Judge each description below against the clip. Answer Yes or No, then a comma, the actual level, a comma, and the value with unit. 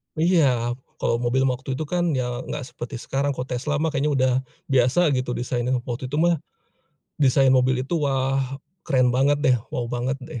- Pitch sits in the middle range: No, low, 130 Hz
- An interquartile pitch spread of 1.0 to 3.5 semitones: Yes, narrow, 2.4 semitones